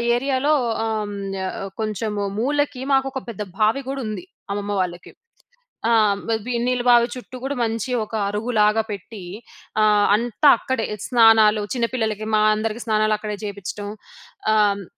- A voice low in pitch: No, high, 220 Hz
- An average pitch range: Yes, average, 3.0 semitones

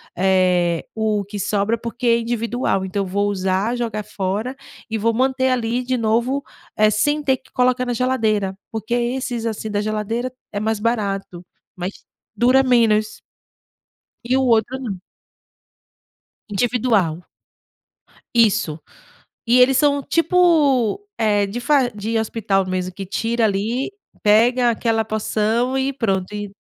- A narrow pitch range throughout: No, average, 3.4 semitones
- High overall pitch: Yes, high, 225 Hz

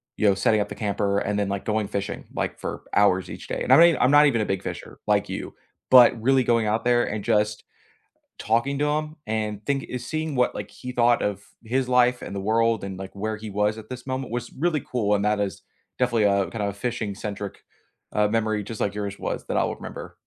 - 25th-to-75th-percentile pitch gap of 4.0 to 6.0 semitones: No, average, 3.3 semitones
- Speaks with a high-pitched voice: No, low, 110 Hz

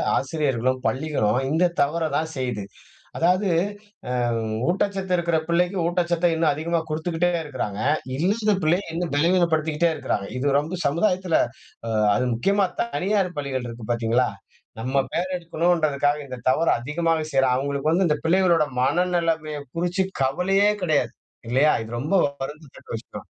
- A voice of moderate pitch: Yes, medium, 160 Hz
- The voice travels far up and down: No, average, 4.2 semitones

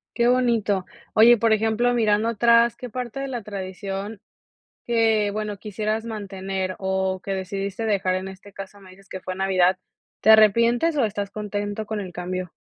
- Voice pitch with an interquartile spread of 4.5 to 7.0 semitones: No, average, 2.9 semitones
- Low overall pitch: No, high, 205 Hz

